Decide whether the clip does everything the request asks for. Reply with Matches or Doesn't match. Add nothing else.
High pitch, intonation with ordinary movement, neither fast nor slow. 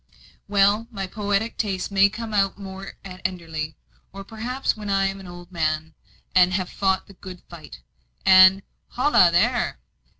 Doesn't match